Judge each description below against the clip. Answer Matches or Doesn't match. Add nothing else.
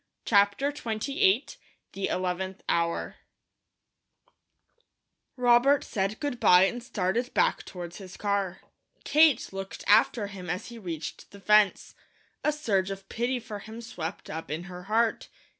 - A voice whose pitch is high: Matches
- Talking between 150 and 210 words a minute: Doesn't match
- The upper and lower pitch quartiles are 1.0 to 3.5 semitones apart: Doesn't match